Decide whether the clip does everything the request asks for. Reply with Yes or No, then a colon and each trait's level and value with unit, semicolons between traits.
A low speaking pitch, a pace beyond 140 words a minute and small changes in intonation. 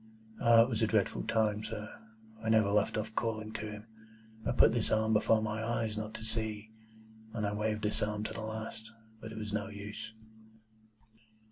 Yes: low, 110 Hz; average, 195 wpm; narrow, 0.8 semitones